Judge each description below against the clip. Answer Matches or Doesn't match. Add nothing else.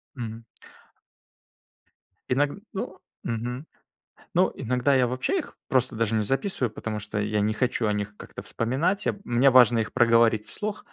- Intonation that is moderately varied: Matches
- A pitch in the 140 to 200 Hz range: Doesn't match